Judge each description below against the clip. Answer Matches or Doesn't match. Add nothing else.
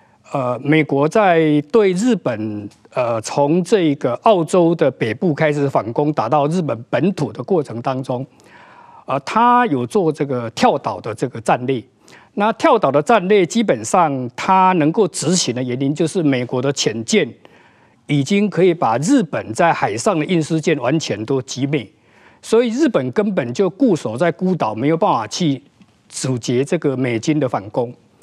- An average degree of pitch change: Doesn't match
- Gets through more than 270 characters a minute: Doesn't match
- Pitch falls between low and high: Matches